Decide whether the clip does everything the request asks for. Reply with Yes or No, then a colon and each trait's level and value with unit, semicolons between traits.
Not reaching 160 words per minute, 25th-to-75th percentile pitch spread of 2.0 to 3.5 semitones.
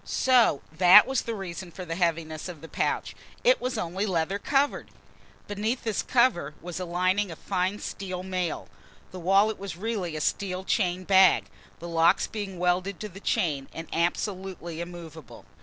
No: average, 170 wpm; average, 3.0 semitones